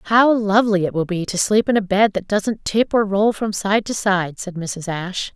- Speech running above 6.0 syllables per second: No, 4.9 syllables/s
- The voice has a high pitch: Yes, high, 200 Hz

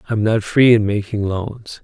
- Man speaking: Yes, male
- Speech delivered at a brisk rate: No, average, 195 wpm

